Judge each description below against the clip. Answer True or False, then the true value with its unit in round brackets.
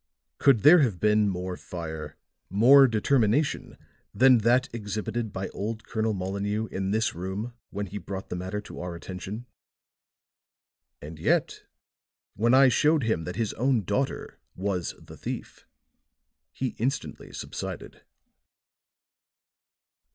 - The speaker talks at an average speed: False (125 wpm)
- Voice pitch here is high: False (105 Hz)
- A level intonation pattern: False (4.2 semitones)